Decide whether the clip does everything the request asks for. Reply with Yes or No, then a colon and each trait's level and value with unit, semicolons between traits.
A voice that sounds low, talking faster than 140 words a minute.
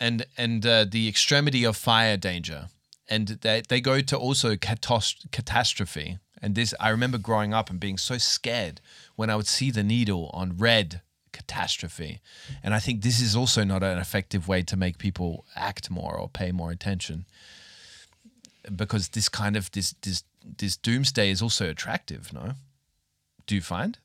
Yes: low, 105 Hz; average, 170 wpm